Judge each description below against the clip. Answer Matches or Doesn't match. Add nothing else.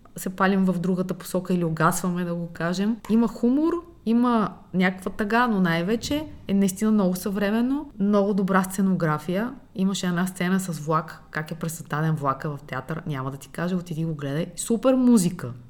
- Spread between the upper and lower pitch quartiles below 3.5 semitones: Doesn't match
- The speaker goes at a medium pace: Doesn't match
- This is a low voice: Doesn't match